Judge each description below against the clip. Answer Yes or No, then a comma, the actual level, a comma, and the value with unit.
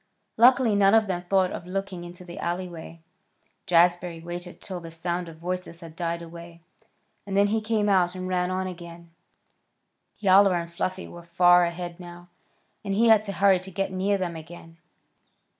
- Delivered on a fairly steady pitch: Yes, narrow, 2.1 semitones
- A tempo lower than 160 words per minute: No, average, 175 wpm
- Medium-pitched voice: Yes, medium, 180 Hz